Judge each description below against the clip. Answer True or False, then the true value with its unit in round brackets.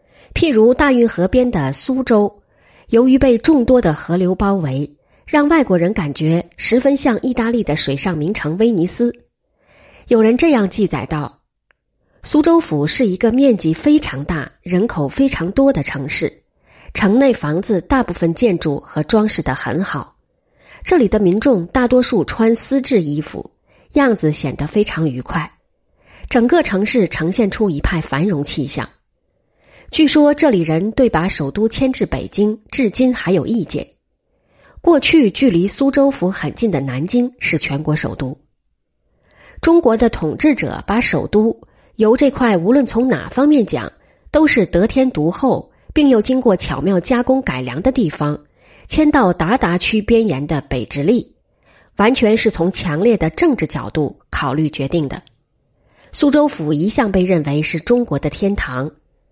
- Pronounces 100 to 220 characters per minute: False (230 characters per minute)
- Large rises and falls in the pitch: True (8.1 semitones)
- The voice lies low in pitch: False (210 Hz)